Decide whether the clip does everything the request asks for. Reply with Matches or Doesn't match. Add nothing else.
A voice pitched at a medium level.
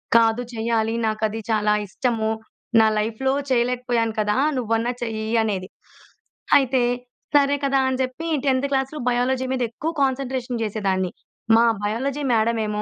Doesn't match